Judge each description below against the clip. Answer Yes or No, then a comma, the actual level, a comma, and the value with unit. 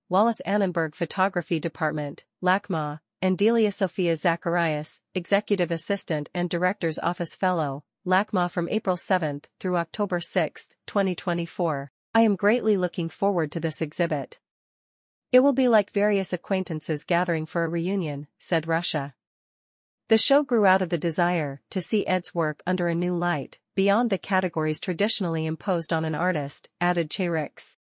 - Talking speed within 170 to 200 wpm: No, average, 150 wpm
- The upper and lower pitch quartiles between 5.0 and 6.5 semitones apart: No, average, 3.1 semitones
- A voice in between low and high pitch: Yes, medium, 175 Hz